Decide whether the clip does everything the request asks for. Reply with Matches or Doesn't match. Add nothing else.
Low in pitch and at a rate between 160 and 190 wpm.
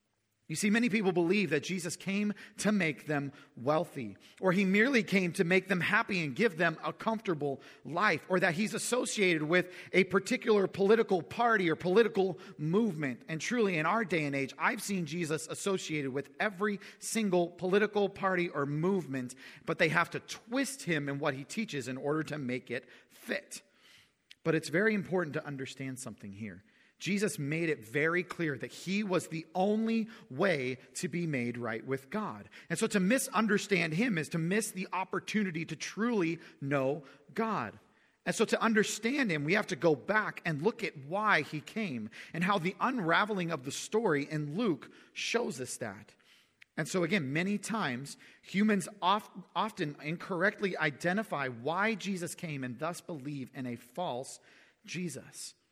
Doesn't match